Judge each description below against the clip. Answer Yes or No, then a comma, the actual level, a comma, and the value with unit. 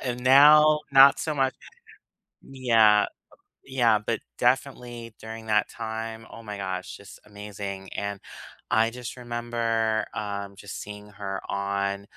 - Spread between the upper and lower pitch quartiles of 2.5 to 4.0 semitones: Yes, average, 3.2 semitones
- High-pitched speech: No, low, 110 Hz